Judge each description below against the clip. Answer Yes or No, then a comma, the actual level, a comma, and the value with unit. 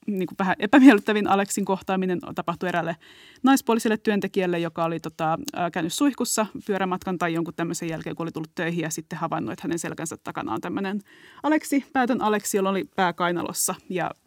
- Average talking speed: No, fast, 170 wpm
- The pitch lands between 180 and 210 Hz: Yes, medium, 185 Hz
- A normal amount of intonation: Yes, average, 4.0 semitones